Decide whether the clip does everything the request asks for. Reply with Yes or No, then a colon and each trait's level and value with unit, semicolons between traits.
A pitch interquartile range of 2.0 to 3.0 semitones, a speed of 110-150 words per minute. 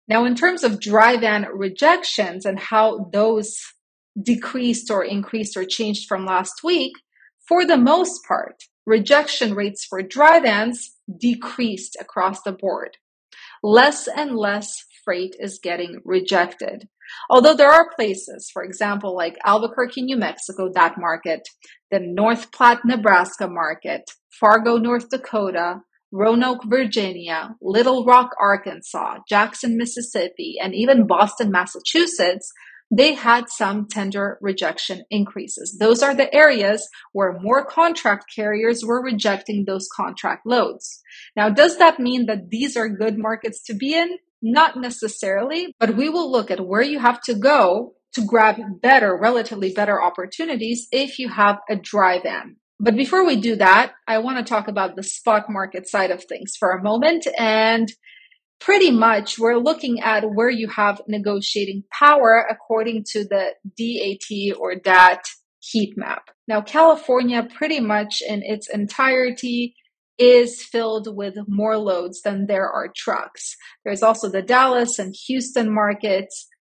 No: average, 3.6 semitones; average, 145 wpm